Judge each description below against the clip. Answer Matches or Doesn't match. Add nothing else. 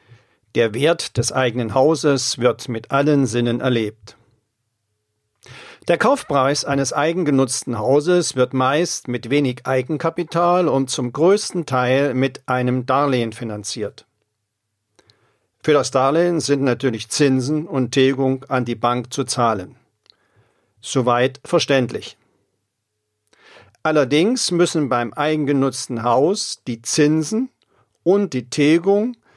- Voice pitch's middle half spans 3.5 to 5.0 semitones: Matches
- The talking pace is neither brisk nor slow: Doesn't match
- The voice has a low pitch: Matches